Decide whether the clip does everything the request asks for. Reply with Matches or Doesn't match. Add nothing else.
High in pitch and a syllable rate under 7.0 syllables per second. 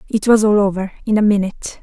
Matches